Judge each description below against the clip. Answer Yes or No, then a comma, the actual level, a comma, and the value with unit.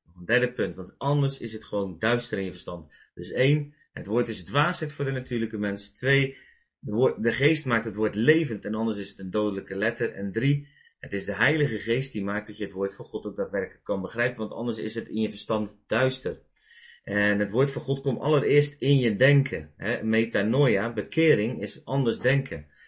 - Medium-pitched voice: No, low, 115 Hz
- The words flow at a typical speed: No, fast, 210 wpm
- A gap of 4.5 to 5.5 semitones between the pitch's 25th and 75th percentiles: Yes, average, 4.9 semitones